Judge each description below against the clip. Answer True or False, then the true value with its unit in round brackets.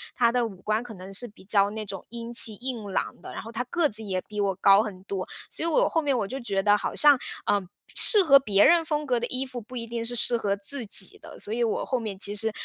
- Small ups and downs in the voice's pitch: False (3.7 semitones)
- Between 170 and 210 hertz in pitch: False (225 Hz)